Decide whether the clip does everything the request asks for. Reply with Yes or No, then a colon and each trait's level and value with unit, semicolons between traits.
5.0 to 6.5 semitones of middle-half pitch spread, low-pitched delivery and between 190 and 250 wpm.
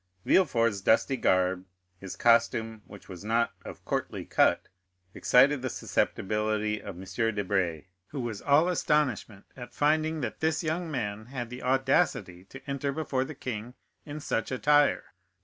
No: average, 5.3 semitones; low, 120 Hz; average, 150 wpm